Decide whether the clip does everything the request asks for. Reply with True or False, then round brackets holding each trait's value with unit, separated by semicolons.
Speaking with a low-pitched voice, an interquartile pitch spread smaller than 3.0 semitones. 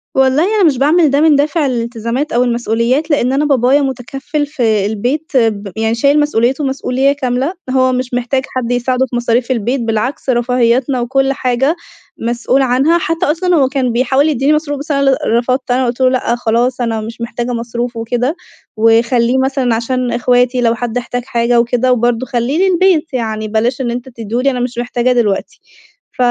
False (250 Hz; 2.5 semitones)